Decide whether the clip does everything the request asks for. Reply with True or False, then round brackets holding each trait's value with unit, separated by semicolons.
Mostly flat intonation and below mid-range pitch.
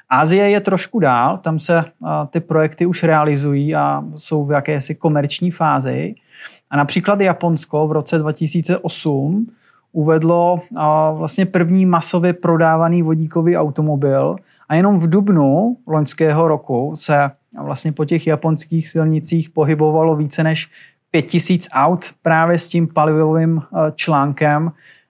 False (2.1 semitones; 160 Hz)